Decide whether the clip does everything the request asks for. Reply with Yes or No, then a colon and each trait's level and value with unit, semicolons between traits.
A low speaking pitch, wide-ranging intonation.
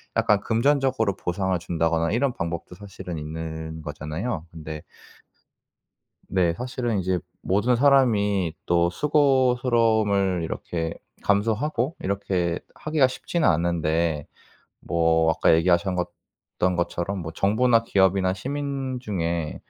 Yes: very low, 95 Hz; wide, 6.1 semitones